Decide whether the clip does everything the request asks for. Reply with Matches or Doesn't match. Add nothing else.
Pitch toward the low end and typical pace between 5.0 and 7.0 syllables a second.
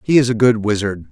Matches